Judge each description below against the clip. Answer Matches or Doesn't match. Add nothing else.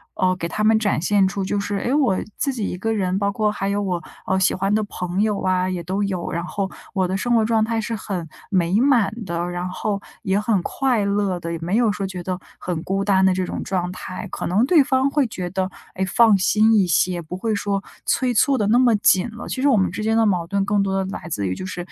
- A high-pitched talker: Matches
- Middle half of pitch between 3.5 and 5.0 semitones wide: Doesn't match